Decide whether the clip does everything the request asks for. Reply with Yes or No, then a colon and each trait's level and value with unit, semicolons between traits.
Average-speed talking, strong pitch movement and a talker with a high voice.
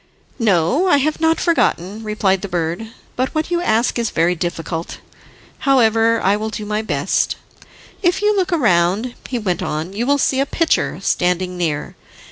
Yes: average, 170 wpm; wide, 7.4 semitones; high, 220 Hz